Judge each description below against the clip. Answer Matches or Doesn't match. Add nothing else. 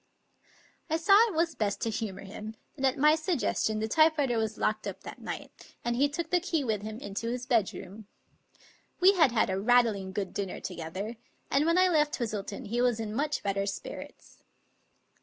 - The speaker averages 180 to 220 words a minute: Matches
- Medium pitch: Doesn't match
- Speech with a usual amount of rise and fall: Doesn't match